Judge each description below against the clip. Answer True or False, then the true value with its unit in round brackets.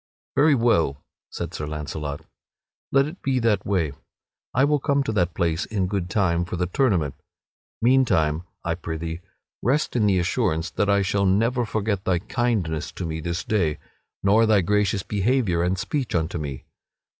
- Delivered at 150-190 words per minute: True (170 wpm)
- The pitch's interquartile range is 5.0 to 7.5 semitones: True (5.5 semitones)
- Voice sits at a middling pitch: False (95 Hz)